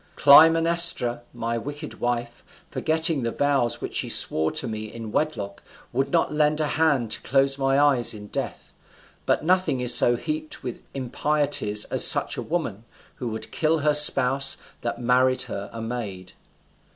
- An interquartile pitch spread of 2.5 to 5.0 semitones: Yes, average, 4.3 semitones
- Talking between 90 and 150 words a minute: No, average, 165 wpm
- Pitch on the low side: Yes, low, 130 Hz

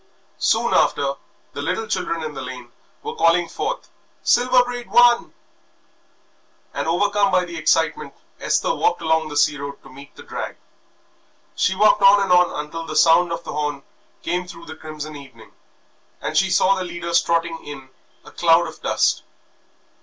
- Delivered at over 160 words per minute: Yes, average, 170 wpm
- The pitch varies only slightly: No, average, 3.9 semitones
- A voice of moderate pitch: Yes, medium, 170 Hz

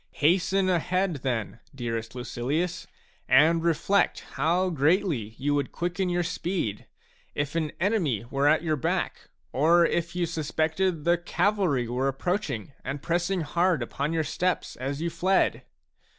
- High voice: No, medium, 160 Hz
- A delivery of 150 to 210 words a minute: No, average, 140 wpm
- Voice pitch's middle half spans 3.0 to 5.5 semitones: Yes, average, 4.4 semitones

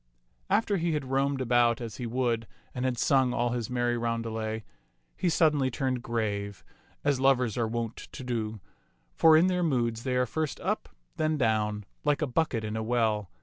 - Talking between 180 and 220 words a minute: Yes, average, 185 wpm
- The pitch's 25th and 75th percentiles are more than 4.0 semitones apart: No, average, 3.3 semitones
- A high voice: No, low, 120 Hz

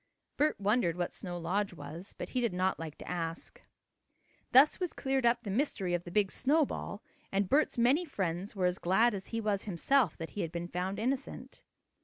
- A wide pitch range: Yes, wide, 5.7 semitones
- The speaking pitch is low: No, high, 200 Hz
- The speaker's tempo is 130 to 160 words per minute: No, average, 200 wpm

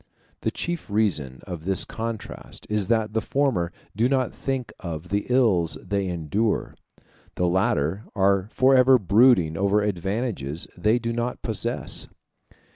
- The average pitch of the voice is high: No, low, 105 Hz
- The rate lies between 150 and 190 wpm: No, slow, 135 wpm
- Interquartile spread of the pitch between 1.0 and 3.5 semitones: No, average, 4.8 semitones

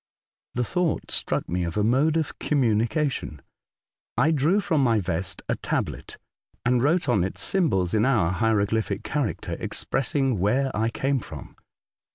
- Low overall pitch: Yes, low, 120 Hz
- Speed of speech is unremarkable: Yes, average, 155 wpm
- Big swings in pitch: Yes, wide, 5.9 semitones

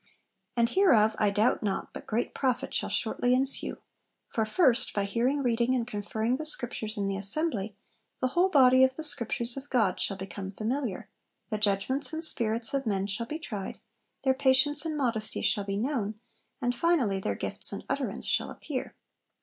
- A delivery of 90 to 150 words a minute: No, average, 180 wpm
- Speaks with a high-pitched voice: Yes, high, 235 Hz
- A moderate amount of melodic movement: Yes, average, 4.3 semitones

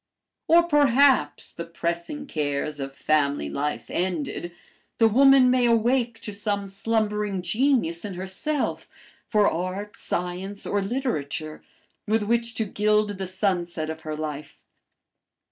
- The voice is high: Yes, high, 200 Hz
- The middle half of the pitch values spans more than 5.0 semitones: Yes, wide, 5.6 semitones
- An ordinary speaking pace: No, slow, 130 wpm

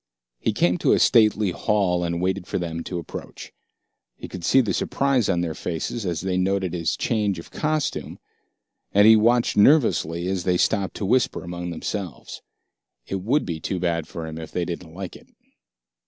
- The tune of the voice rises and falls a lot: No, average, 3.7 semitones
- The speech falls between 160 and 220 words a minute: Yes, average, 185 wpm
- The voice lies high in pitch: No, very low, 90 Hz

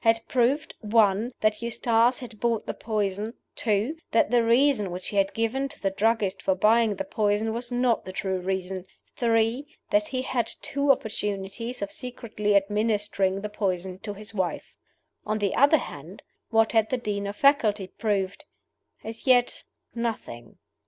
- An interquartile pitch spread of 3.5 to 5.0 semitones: No, average, 3.0 semitones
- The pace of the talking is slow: No, average, 165 wpm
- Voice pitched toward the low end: No, high, 220 Hz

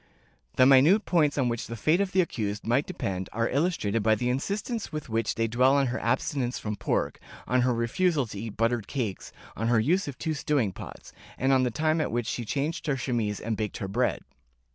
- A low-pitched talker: Yes, low, 125 Hz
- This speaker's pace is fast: Yes, fast, 220 wpm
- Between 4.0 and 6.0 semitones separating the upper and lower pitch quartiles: Yes, average, 4.8 semitones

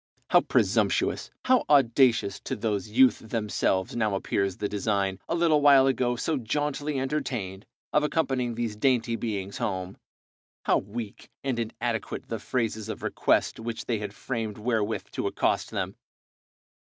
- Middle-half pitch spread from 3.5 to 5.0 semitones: Yes, average, 4.1 semitones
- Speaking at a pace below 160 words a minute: Yes, average, 145 wpm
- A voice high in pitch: No, low, 115 Hz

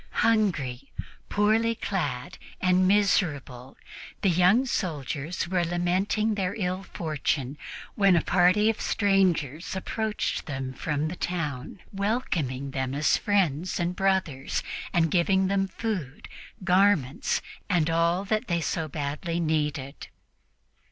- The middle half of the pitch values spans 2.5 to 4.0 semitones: No, average, 4.7 semitones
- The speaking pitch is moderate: Yes, medium, 175 Hz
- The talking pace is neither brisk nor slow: No, slow, 120 wpm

